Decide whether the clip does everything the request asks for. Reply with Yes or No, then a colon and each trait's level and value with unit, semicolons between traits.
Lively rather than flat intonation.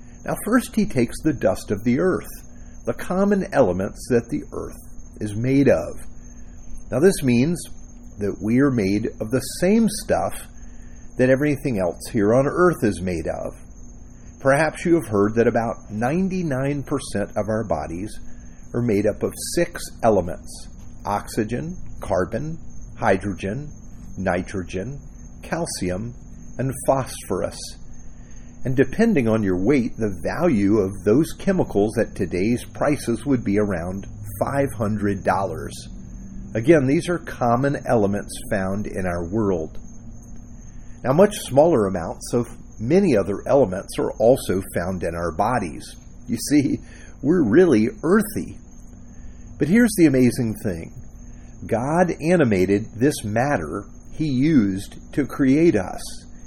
Yes: wide, 6.2 semitones